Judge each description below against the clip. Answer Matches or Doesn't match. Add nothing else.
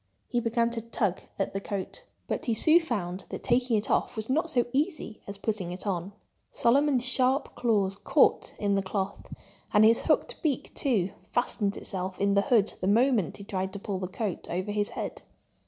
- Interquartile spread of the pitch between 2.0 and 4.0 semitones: Matches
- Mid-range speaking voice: Doesn't match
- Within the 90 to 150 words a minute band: Doesn't match